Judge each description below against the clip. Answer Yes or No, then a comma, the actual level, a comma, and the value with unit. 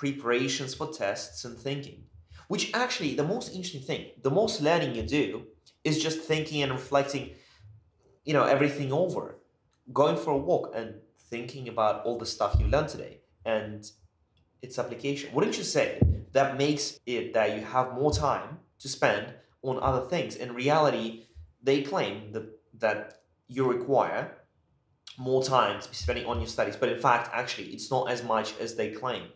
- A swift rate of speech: No, average, 170 wpm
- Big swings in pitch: No, average, 4.6 semitones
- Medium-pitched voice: No, low, 130 Hz